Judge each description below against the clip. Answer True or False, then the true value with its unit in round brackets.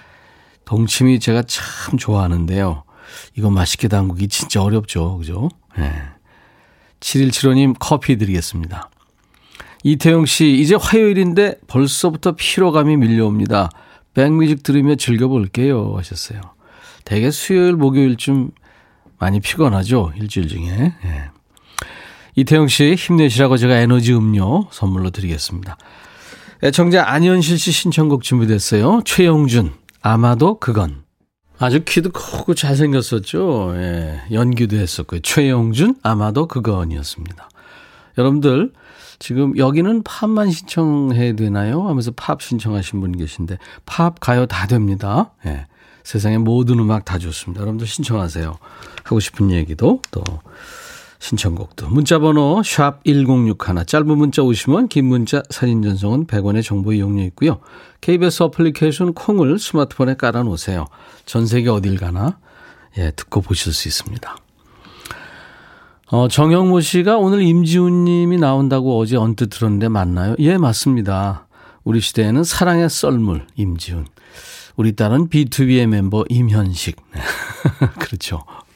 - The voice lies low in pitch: True (120 Hz)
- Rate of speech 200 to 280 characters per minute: False (290 characters per minute)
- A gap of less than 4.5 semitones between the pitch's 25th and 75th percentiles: False (7.2 semitones)